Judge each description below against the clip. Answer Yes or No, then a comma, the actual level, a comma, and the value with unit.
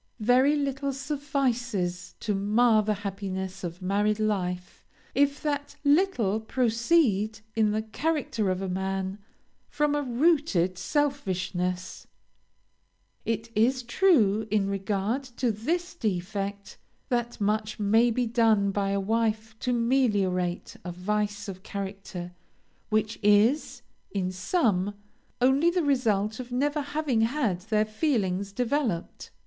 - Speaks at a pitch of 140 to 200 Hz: No, high, 215 Hz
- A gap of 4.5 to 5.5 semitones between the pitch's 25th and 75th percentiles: Yes, average, 4.8 semitones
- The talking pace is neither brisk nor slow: No, slow, 120 wpm